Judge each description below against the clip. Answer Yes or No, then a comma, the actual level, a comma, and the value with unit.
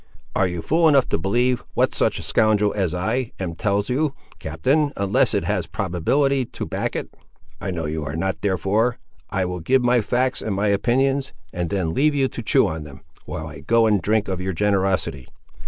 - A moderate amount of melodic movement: No, wide, 5.8 semitones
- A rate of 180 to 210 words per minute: Yes, fast, 205 wpm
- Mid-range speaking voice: No, low, 100 Hz